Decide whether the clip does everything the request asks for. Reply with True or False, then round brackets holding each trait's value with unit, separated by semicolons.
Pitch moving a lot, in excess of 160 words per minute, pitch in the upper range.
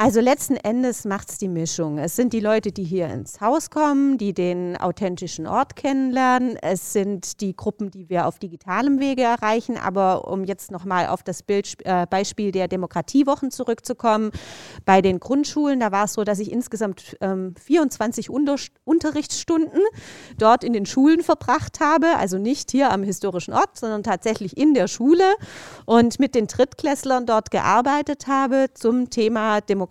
True (5.9 semitones; 170 wpm; 220 Hz)